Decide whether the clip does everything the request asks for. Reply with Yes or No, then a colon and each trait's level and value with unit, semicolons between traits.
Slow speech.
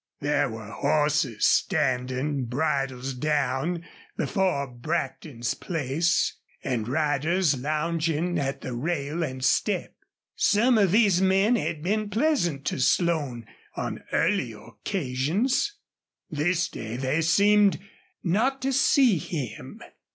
Yes: slow, 110 wpm